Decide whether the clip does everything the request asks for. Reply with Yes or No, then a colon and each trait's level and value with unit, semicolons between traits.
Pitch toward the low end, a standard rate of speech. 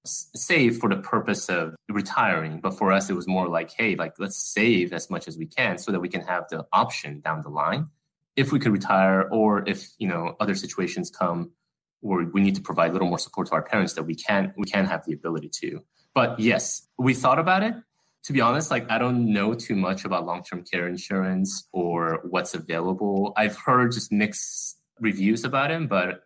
No: low, 100 Hz; fast, 215 wpm